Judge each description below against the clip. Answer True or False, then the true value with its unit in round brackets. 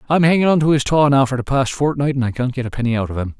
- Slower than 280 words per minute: False (355 wpm)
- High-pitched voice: False (135 Hz)